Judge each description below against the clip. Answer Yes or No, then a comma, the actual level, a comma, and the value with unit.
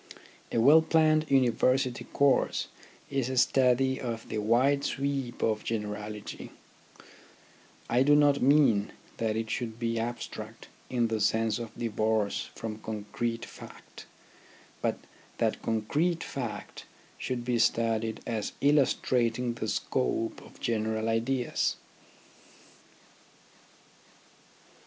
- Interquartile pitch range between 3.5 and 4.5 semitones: No, average, 3.1 semitones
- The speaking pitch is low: Yes, low, 120 Hz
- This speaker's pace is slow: Yes, slow, 110 wpm